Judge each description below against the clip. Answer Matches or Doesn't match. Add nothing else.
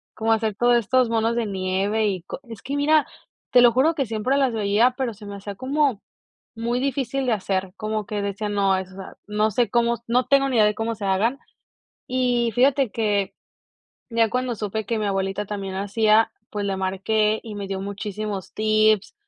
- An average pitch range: Matches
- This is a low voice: Doesn't match